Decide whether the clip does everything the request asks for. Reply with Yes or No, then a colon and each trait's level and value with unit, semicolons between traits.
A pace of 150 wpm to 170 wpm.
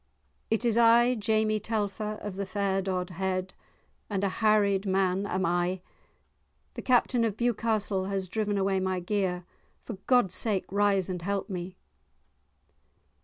No: average, 140 wpm